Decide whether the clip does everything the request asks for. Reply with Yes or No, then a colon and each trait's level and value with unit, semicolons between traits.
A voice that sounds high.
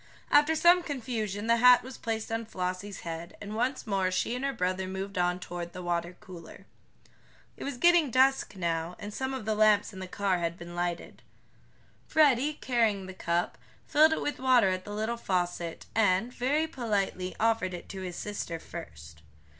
Yes: high, 205 Hz